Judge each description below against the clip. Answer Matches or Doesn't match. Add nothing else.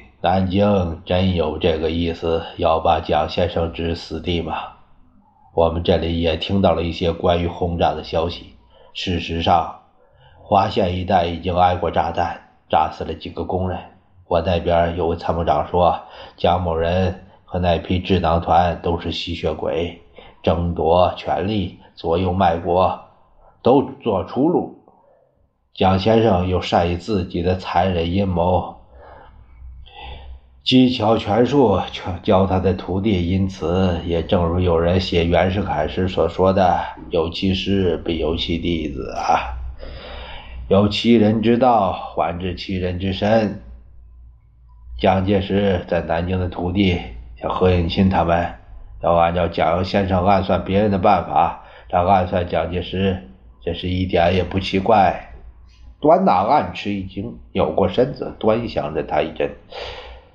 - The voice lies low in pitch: Matches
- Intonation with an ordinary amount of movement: Doesn't match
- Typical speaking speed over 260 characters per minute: Doesn't match